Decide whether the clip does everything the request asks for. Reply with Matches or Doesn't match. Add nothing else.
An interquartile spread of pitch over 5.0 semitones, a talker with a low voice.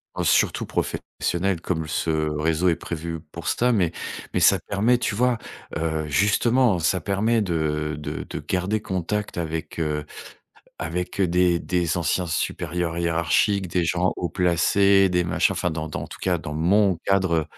Doesn't match